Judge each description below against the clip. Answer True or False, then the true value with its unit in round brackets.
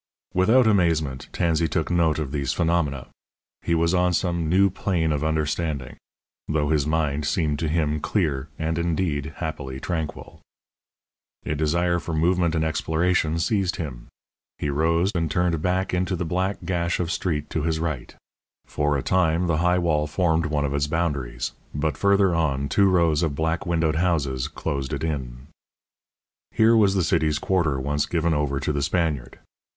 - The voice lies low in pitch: True (80 Hz)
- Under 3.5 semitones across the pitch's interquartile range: True (2.8 semitones)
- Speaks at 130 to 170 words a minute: True (165 wpm)